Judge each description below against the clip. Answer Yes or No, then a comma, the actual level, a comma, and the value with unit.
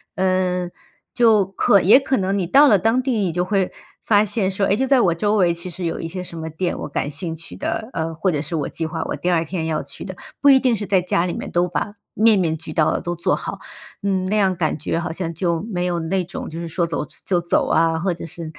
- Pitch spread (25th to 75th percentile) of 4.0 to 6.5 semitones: No, average, 3.2 semitones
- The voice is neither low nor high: Yes, medium, 180 Hz